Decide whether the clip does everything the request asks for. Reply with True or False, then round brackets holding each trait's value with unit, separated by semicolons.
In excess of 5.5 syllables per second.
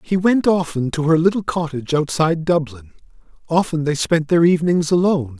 True (5.7 syllables/s)